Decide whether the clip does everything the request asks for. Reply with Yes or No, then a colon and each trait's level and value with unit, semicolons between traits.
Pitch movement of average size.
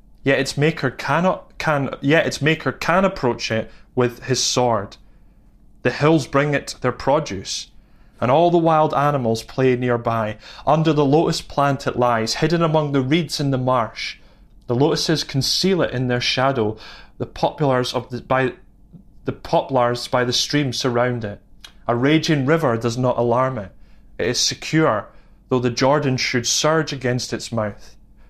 Yes: average, 3.5 semitones